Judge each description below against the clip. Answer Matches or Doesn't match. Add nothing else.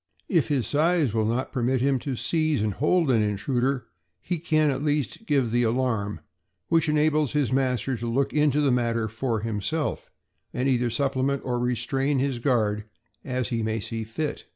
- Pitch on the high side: Doesn't match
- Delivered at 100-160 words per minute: Doesn't match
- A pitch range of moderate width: Matches